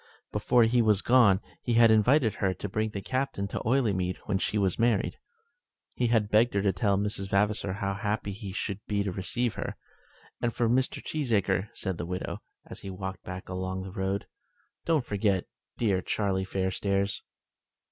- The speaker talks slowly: No, average, 175 wpm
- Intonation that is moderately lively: Yes, average, 3.0 semitones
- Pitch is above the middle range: No, low, 100 Hz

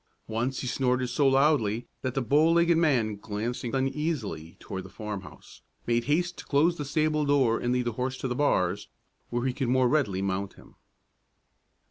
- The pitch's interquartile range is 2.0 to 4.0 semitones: No, average, 4.4 semitones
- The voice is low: Yes, low, 125 Hz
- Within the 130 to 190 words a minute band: Yes, average, 180 wpm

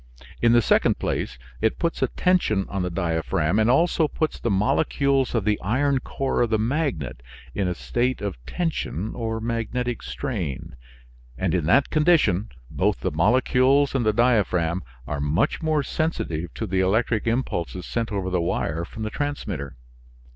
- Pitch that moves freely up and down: Yes, wide, 6.5 semitones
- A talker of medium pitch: No, low, 110 Hz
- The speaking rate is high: No, average, 165 wpm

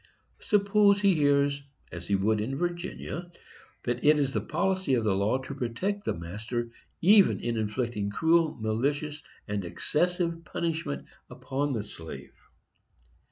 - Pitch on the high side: No, medium, 140 Hz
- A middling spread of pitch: No, wide, 7.7 semitones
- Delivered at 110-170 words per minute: Yes, average, 140 wpm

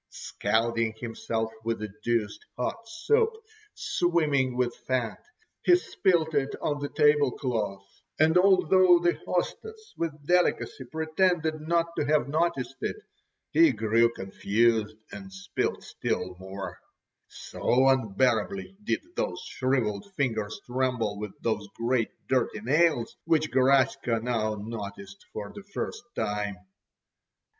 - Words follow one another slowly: Yes, slow, 120 wpm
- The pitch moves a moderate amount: No, wide, 7.0 semitones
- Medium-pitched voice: No, low, 130 Hz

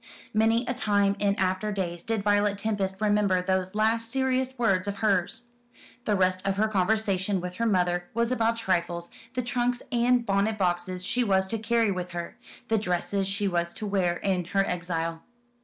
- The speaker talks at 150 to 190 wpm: Yes, average, 180 wpm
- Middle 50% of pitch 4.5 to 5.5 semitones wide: No, average, 3.4 semitones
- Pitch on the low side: No, high, 200 Hz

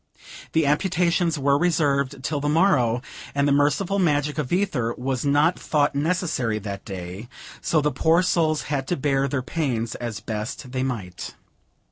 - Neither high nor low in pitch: Yes, medium, 145 Hz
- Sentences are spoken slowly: No, average, 160 wpm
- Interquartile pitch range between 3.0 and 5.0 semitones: Yes, average, 4.3 semitones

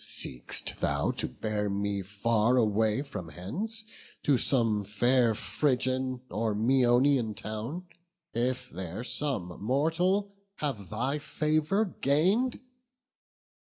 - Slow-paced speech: Yes, slow, 105 wpm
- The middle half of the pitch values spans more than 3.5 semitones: Yes, wide, 5.5 semitones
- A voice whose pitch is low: Yes, low, 125 Hz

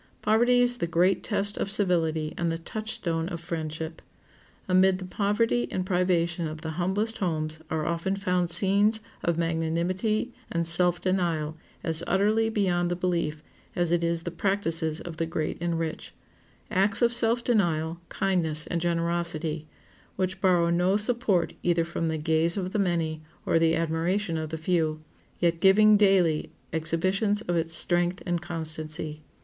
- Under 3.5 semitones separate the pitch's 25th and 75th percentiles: Yes, average, 2.9 semitones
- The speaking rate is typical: Yes, average, 155 wpm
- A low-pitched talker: No, medium, 175 Hz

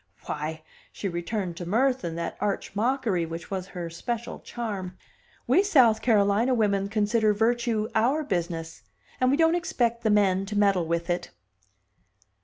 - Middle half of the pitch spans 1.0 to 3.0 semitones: No, average, 4.8 semitones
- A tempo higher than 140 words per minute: Yes, average, 155 wpm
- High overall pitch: Yes, high, 205 Hz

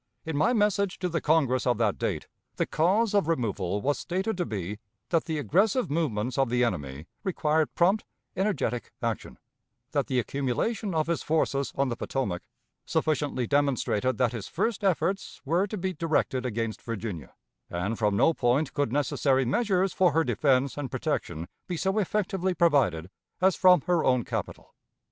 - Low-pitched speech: No, medium, 145 Hz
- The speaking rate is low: No, average, 165 wpm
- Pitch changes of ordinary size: No, wide, 6.9 semitones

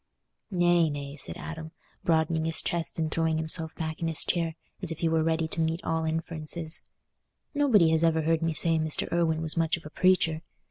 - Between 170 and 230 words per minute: Yes, average, 200 wpm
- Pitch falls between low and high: Yes, medium, 160 Hz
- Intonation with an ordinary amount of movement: No, narrow, 0.9 semitones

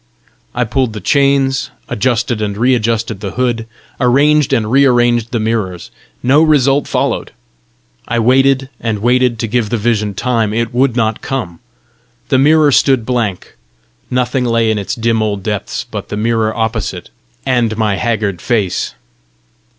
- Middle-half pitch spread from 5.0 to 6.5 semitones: No, average, 2.8 semitones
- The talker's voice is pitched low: Yes, low, 115 Hz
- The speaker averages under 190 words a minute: Yes, average, 155 wpm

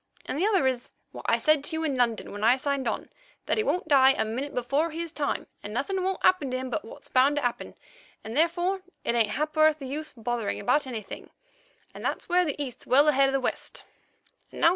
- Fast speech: Yes, fast, 230 wpm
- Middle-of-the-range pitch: No, very high, 275 Hz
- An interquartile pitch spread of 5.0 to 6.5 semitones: No, average, 4.0 semitones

